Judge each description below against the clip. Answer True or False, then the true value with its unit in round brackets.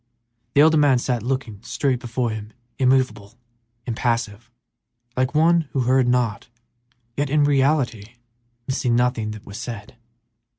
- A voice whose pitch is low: True (125 Hz)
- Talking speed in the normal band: False (130 wpm)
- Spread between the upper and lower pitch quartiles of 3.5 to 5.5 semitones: False (3.1 semitones)